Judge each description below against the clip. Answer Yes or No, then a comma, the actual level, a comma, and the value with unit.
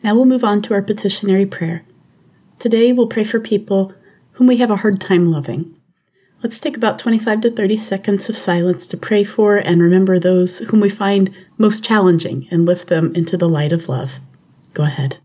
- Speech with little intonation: No, average, 3.7 semitones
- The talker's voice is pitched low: No, high, 195 Hz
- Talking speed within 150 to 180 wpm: No, average, 195 wpm